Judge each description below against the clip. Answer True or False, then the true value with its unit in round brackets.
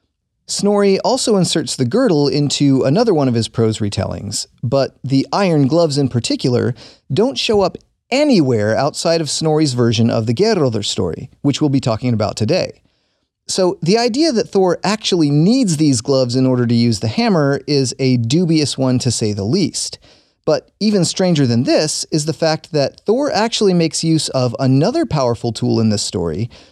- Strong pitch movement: True (6.2 semitones)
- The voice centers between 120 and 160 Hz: True (140 Hz)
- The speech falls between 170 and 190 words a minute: True (175 wpm)